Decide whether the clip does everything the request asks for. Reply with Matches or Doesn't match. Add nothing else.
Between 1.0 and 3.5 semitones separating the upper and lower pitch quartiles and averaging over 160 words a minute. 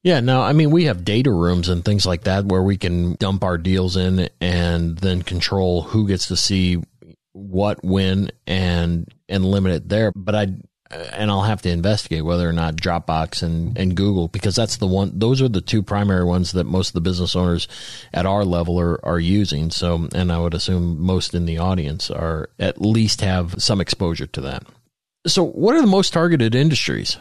Matches